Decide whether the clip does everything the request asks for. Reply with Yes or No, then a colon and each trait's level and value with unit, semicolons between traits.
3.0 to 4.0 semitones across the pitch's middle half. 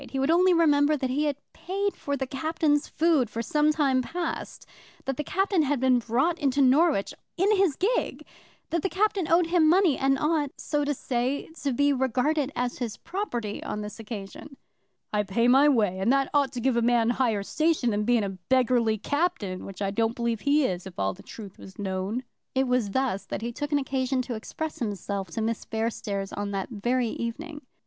No: average, 5.0 semitones